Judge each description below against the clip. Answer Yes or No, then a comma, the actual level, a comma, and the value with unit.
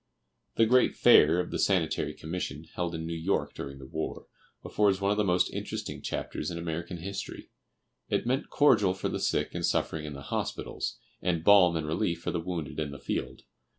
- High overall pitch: No, very low, 85 Hz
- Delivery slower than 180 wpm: No, average, 195 wpm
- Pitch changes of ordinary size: Yes, average, 3.4 semitones